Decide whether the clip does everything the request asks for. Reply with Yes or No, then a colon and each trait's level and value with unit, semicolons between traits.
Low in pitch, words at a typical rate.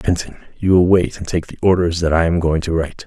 No: very low, 85 Hz; fast, 295 wpm